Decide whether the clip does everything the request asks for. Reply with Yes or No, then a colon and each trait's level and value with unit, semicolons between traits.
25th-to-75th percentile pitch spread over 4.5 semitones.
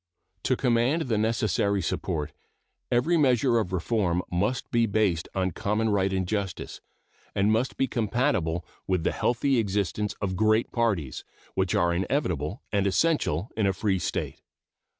No: average, 4.2 semitones